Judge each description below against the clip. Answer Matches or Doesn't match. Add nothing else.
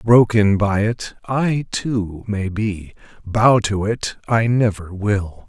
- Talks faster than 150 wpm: Doesn't match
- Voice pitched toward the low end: Matches